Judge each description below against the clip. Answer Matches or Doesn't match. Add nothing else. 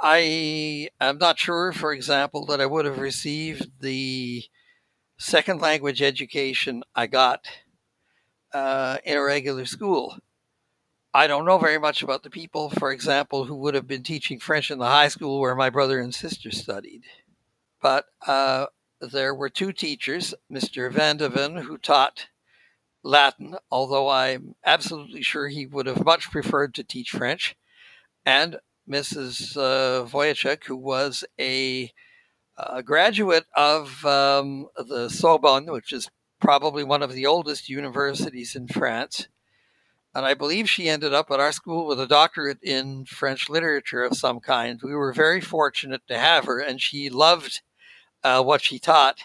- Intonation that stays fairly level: Matches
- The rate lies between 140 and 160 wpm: Matches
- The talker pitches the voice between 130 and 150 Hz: Matches